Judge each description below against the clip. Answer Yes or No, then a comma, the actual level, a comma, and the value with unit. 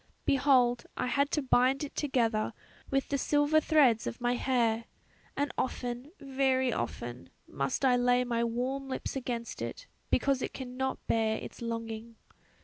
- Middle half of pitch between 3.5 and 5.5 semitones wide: No, narrow, 2.6 semitones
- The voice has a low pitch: No, very high, 250 Hz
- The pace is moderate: Yes, average, 150 wpm